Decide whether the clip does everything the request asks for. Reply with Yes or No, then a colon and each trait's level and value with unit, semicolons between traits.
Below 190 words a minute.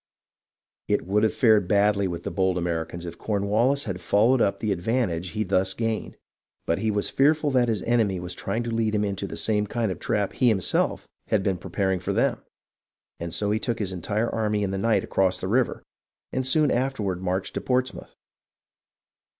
No: average, 200 wpm